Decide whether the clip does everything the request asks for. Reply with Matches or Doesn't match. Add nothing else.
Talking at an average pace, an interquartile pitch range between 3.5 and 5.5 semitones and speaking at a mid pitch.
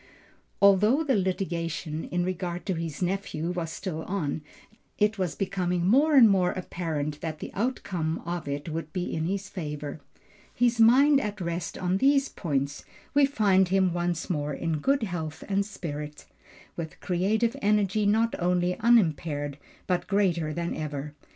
Matches